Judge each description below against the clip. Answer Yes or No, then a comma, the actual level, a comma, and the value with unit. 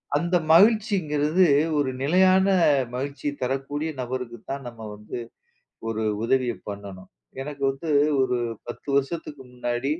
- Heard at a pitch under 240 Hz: Yes, low, 135 Hz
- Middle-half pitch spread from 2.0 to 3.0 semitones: No, average, 4.3 semitones